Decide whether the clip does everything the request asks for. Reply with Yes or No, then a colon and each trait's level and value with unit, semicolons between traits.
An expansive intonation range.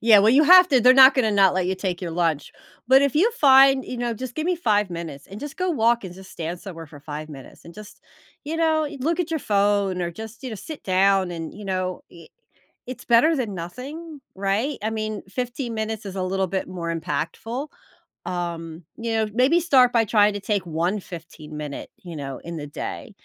Yes: wide, 6.6 semitones